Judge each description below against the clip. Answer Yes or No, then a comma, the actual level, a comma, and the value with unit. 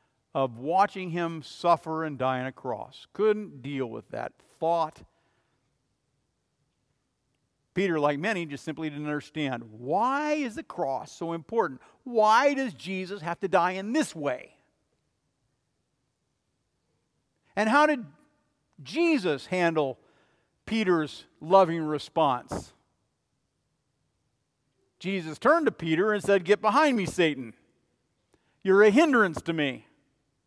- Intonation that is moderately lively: No, wide, 6.2 semitones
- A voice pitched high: No, medium, 170 Hz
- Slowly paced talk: Yes, slow, 115 wpm